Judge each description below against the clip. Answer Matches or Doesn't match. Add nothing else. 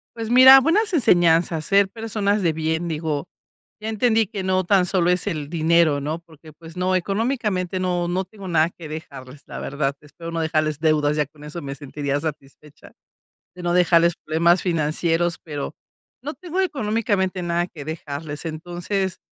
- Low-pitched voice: Doesn't match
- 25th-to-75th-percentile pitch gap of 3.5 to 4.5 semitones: Matches